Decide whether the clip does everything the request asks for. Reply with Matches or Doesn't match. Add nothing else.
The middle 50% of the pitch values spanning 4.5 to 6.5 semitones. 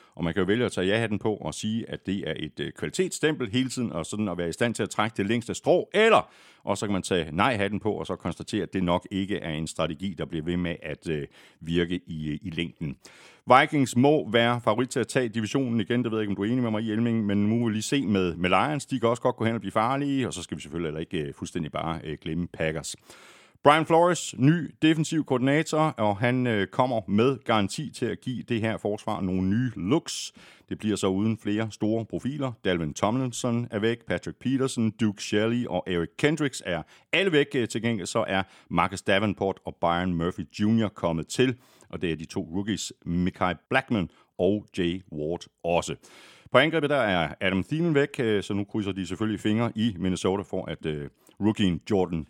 Matches